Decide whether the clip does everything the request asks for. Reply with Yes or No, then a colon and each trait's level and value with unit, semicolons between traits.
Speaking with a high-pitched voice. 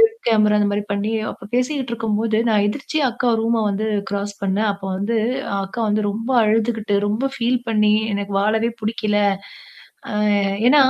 Yes: high, 215 Hz